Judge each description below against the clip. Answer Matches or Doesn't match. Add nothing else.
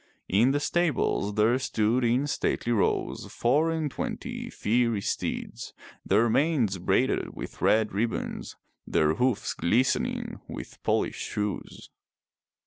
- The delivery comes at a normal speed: Doesn't match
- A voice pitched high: Doesn't match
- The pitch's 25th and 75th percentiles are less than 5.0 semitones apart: Matches